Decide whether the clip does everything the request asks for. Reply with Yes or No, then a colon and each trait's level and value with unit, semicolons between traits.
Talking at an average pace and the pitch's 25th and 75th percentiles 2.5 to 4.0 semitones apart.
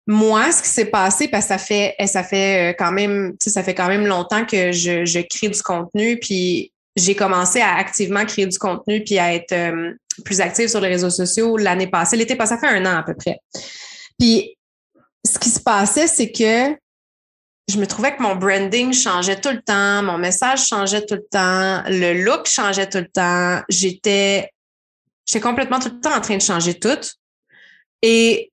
Yes: average, 195 wpm; average, 3.5 semitones